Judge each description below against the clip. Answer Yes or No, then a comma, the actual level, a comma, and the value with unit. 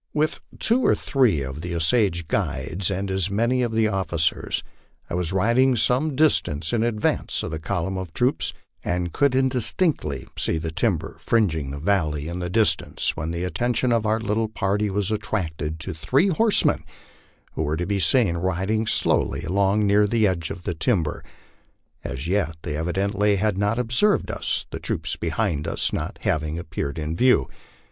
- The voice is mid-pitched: No, very low, 95 Hz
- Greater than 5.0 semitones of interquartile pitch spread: Yes, wide, 5.4 semitones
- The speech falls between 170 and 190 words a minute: Yes, average, 180 wpm